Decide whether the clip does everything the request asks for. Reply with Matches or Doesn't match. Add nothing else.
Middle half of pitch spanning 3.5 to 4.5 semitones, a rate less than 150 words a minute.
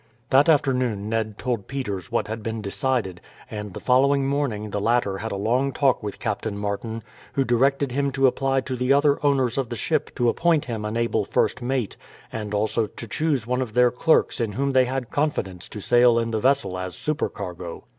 Doesn't match